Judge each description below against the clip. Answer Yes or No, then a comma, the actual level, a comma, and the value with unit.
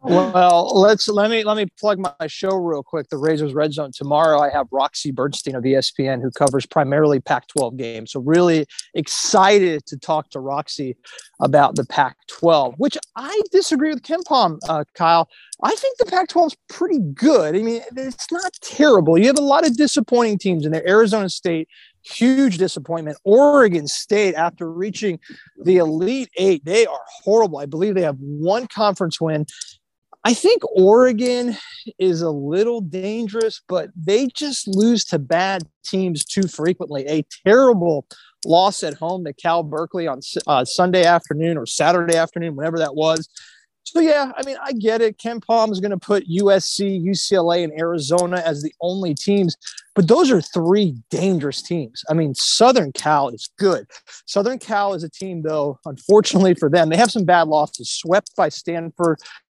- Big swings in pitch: Yes, wide, 5.9 semitones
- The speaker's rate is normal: Yes, average, 170 wpm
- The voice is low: No, medium, 180 Hz